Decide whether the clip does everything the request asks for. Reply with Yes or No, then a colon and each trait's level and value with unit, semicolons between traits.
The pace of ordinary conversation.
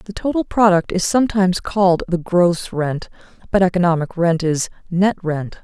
Yes: average, 160 wpm